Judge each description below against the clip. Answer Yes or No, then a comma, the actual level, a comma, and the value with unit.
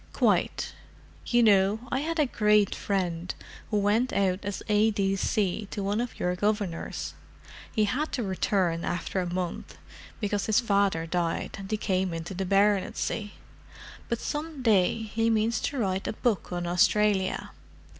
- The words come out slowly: No, average, 155 wpm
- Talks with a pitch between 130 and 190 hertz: No, high, 205 Hz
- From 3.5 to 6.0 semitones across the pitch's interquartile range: No, average, 2.9 semitones